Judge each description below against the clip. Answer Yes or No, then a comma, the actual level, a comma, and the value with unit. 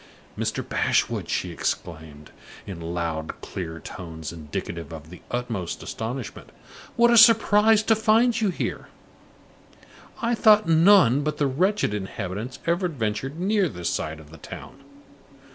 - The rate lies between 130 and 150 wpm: Yes, slow, 135 wpm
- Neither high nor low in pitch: No, low, 125 Hz